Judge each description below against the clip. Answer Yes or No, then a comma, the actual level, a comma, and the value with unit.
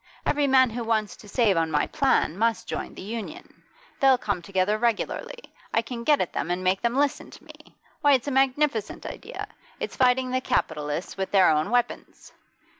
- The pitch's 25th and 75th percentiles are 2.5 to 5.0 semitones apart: No, wide, 5.4 semitones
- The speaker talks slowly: No, average, 190 wpm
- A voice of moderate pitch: No, high, 230 Hz